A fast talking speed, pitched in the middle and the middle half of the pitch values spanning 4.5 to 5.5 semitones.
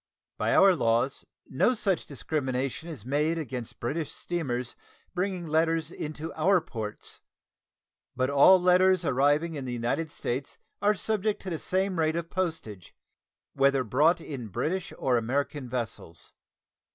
No: average, 140 wpm; medium, 155 Hz; average, 5.2 semitones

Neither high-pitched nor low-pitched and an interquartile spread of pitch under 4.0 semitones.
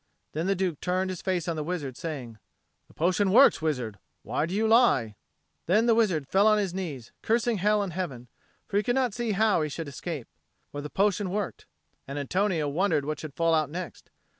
No: medium, 180 Hz; wide, 5.4 semitones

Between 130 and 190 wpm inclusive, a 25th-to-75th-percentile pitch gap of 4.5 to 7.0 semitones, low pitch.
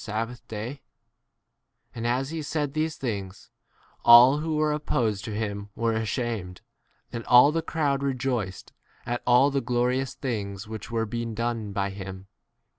No: average, 160 wpm; average, 4.1 semitones; low, 120 Hz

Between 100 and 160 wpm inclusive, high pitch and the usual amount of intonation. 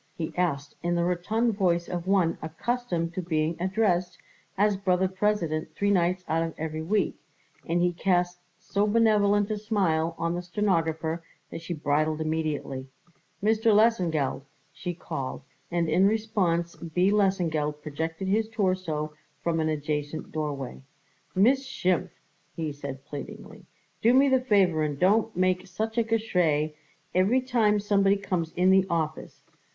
No: average, 150 wpm; medium, 180 Hz; average, 4.2 semitones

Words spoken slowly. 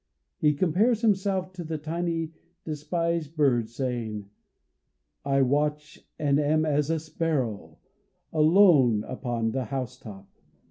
Yes: slow, 110 wpm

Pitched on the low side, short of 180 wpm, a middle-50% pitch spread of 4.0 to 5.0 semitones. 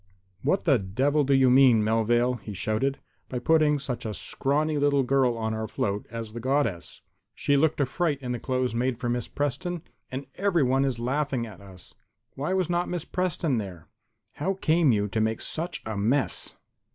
No: low, 130 Hz; average, 190 wpm; average, 4.6 semitones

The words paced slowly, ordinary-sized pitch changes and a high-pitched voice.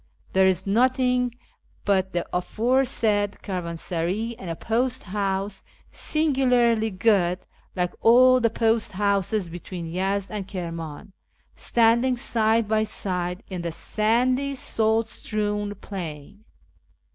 Yes: slow, 110 wpm; average, 3.8 semitones; high, 205 Hz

